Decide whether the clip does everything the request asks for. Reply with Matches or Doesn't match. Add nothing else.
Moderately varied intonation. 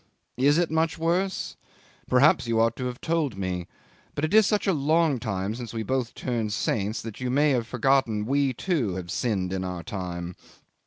Doesn't match